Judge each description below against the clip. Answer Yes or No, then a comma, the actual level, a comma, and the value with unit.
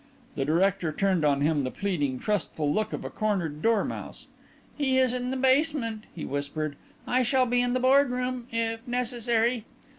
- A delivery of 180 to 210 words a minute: No, average, 170 wpm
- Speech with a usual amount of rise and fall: No, wide, 7.6 semitones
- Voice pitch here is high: Yes, high, 225 Hz